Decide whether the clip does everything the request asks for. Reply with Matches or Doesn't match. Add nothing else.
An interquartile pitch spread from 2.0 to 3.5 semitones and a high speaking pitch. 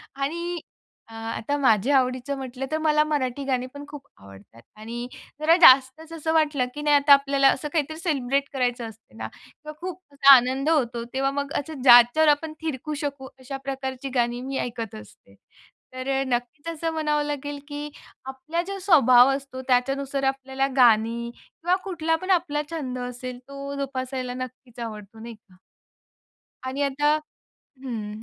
Matches